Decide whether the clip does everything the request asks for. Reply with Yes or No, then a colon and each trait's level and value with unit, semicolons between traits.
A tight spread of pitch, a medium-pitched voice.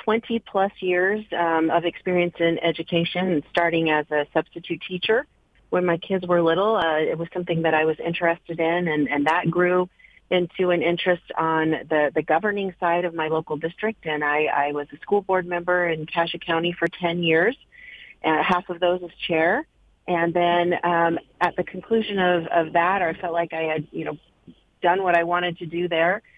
Yes: narrow, 1.7 semitones; medium, 170 Hz